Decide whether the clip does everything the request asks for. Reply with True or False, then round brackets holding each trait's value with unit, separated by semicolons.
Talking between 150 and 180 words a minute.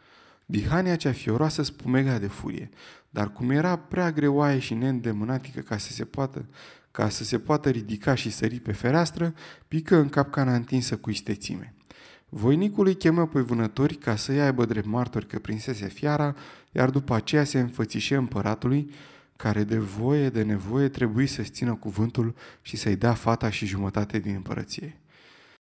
True (160 wpm)